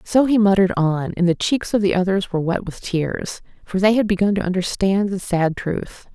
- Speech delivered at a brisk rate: Yes, fast, 225 wpm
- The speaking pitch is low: No, high, 190 Hz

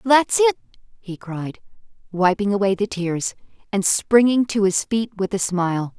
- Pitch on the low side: No, high, 205 Hz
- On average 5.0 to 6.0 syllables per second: No, 4.4 syllables/s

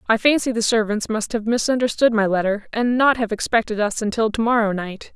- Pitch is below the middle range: No, high, 225 Hz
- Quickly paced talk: Yes, fast, 210 wpm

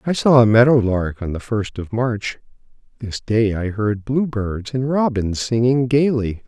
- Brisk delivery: No, average, 185 wpm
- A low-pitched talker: Yes, low, 115 Hz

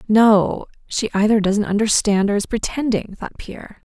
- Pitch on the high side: Yes, high, 210 Hz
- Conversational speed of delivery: Yes, average, 155 wpm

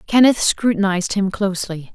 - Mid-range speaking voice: No, high, 200 Hz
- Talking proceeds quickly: No, slow, 125 wpm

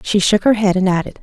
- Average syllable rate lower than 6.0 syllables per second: No, 6.2 syllables/s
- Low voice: No, high, 195 Hz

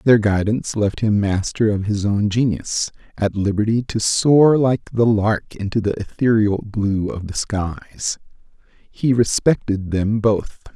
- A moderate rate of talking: Yes, average, 150 wpm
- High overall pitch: No, low, 105 Hz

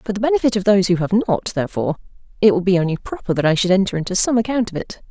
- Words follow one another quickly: Yes, fast, 270 wpm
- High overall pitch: Yes, high, 195 Hz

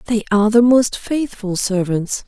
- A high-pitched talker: Yes, high, 215 Hz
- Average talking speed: Yes, average, 160 wpm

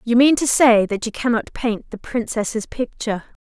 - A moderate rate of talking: Yes, average, 190 wpm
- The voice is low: No, high, 230 Hz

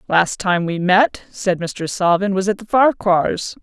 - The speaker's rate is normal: Yes, average, 180 wpm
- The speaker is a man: No, female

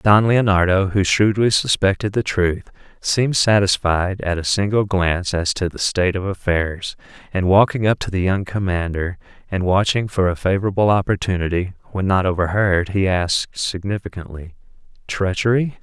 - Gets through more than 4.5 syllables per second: Yes, 5.0 syllables/s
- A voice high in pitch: No, very low, 95 Hz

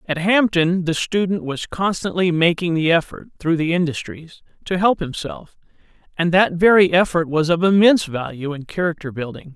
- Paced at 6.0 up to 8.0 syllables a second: No, 5.1 syllables/s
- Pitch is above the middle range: No, medium, 170 Hz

